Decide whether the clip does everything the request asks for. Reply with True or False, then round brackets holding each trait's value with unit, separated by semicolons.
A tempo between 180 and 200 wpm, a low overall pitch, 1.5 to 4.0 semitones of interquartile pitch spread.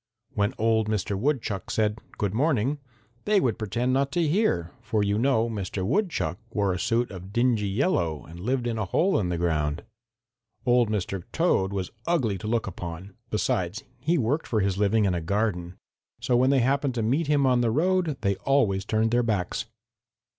False (190 wpm; 110 Hz; 5.2 semitones)